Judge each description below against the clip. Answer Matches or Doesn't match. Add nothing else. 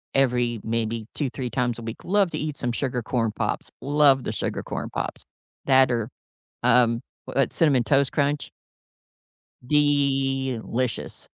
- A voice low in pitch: Matches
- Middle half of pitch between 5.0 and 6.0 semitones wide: Doesn't match